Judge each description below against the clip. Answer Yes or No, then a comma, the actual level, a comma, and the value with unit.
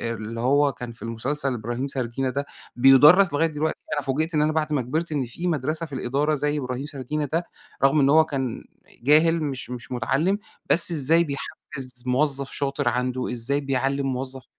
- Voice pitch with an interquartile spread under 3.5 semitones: Yes, average, 3.1 semitones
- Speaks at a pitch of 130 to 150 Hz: Yes, medium, 140 Hz